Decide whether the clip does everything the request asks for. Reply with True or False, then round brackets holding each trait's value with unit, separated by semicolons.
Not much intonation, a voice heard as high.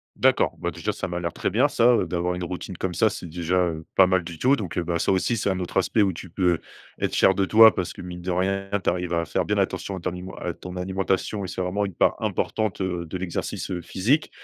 False (1.8 semitones; 90 Hz)